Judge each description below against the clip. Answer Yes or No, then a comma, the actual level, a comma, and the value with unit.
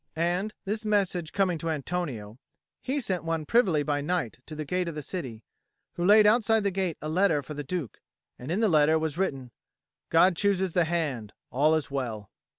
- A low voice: No, medium, 165 Hz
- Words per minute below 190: No, average, 195 wpm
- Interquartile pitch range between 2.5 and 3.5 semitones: No, average, 4.5 semitones